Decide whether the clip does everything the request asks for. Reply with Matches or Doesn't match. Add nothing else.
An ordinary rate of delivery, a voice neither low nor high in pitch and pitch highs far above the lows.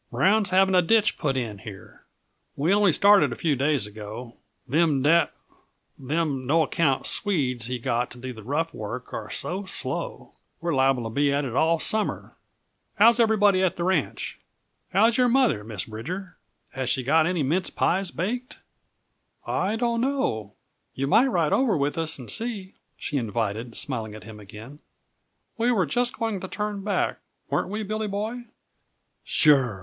Matches